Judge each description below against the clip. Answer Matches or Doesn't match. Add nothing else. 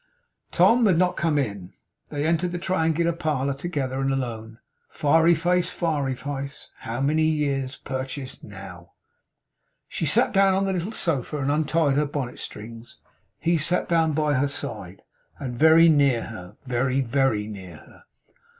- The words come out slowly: Doesn't match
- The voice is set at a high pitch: Doesn't match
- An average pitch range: Matches